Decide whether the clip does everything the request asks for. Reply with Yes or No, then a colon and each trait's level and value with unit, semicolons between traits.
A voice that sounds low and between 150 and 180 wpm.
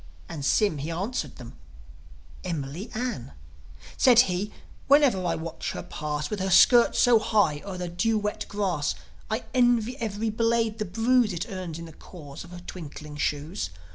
No: high, 190 Hz; average, 170 wpm